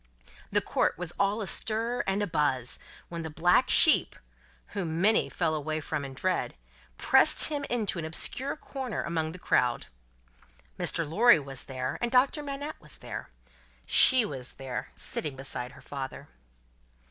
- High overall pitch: No, medium, 170 Hz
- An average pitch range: No, wide, 8.3 semitones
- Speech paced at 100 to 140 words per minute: No, average, 155 wpm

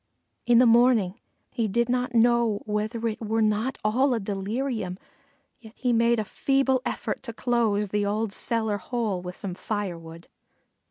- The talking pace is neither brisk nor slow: Yes, average, 160 wpm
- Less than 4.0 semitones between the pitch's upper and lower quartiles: Yes, average, 2.7 semitones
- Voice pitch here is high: Yes, high, 225 Hz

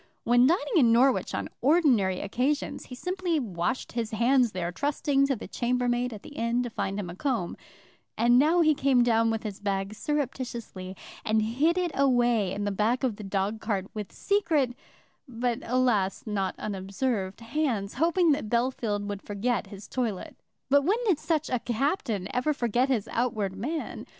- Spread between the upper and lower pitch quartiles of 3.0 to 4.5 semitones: No, average, 4.9 semitones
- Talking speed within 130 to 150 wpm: No, average, 175 wpm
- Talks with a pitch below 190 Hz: No, high, 240 Hz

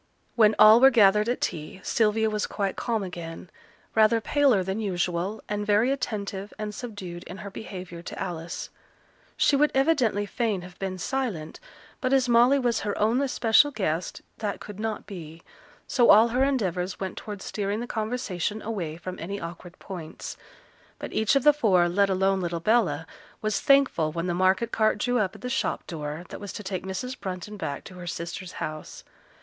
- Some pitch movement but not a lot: Yes, average, 4.2 semitones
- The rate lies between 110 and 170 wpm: No, average, 185 wpm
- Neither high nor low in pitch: No, high, 205 Hz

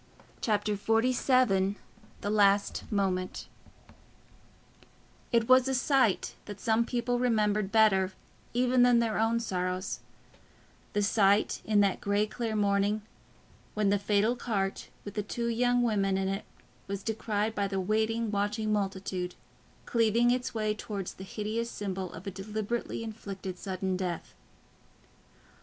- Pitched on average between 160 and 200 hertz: No, high, 210 Hz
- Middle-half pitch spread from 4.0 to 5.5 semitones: No, average, 2.7 semitones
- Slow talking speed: Yes, slow, 130 wpm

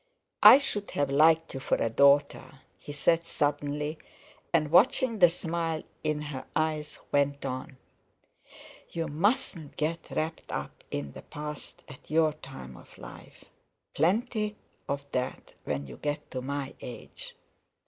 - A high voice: No, medium, 150 Hz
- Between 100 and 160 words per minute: Yes, average, 140 wpm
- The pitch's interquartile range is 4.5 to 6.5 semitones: No, average, 2.8 semitones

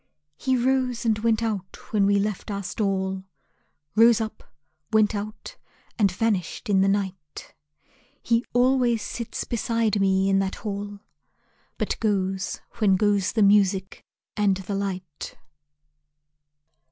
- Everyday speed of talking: No, slow, 130 wpm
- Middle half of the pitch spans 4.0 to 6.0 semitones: No, average, 2.8 semitones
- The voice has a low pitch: No, high, 205 Hz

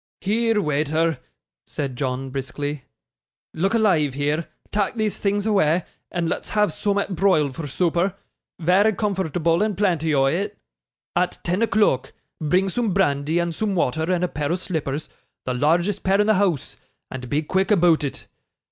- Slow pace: No, average, 160 wpm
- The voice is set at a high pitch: No, medium, 175 Hz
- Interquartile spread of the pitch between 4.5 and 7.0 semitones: Yes, average, 5.0 semitones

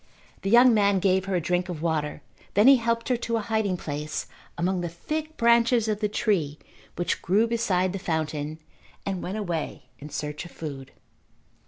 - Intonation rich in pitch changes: Yes, wide, 5.7 semitones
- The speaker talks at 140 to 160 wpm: No, average, 185 wpm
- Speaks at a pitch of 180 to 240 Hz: Yes, high, 190 Hz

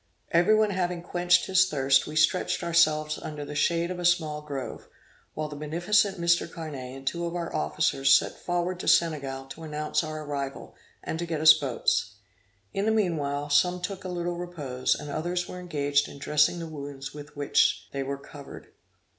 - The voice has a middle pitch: Yes, medium, 155 Hz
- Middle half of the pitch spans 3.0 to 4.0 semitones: Yes, average, 3.6 semitones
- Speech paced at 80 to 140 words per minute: No, average, 190 wpm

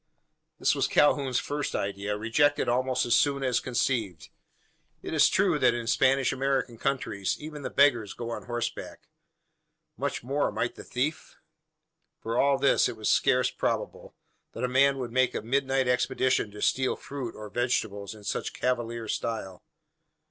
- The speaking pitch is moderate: No, low, 125 Hz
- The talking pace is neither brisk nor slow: Yes, average, 160 wpm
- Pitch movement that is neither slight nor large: Yes, average, 3.0 semitones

